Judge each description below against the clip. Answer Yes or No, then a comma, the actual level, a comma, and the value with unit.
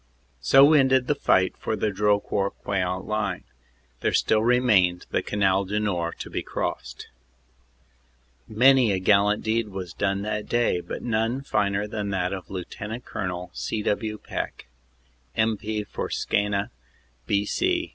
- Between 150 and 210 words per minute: No, average, 140 wpm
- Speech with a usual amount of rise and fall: No, narrow, 2.3 semitones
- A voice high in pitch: No, low, 105 Hz